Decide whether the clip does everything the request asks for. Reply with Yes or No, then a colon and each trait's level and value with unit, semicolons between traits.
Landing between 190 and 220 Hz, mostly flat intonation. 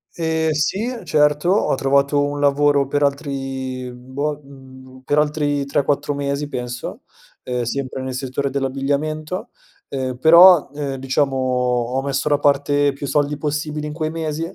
No: medium, 140 Hz; narrow, 2.0 semitones